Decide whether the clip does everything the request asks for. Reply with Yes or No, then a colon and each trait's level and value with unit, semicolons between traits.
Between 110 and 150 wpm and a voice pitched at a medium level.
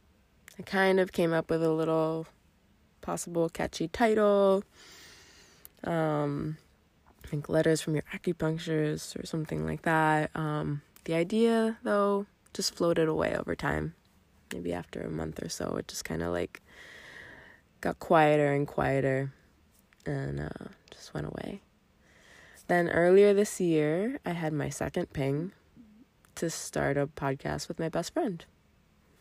Yes: average, 140 wpm; medium, 155 Hz